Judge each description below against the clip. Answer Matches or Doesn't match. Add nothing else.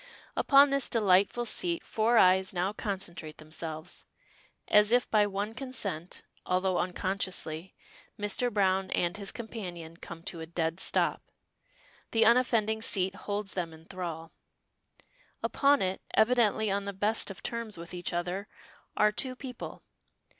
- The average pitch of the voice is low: Doesn't match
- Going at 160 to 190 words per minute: Doesn't match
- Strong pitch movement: Doesn't match